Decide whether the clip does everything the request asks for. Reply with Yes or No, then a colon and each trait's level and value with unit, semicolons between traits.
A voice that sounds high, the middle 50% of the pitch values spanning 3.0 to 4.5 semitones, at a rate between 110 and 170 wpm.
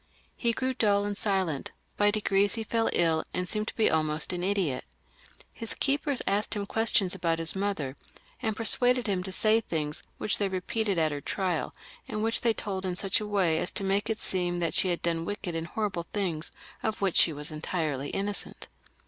No: high, 195 Hz; average, 4.1 semitones; average, 200 wpm